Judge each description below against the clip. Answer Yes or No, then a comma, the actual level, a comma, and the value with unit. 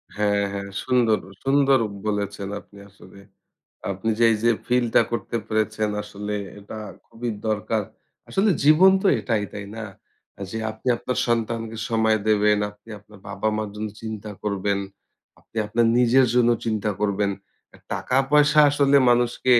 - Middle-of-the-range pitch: No, low, 110 Hz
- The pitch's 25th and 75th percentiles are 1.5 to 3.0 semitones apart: Yes, average, 2.7 semitones